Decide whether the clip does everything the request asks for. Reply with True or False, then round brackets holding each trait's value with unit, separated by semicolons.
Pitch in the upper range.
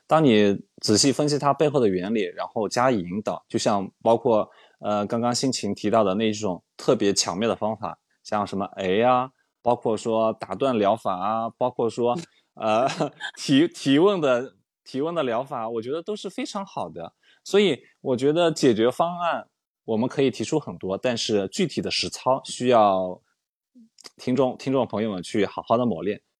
False (120 Hz)